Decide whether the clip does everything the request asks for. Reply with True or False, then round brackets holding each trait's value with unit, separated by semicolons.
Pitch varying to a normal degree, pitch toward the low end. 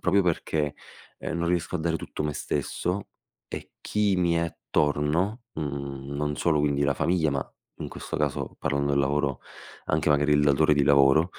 True (3.1 semitones; 75 Hz)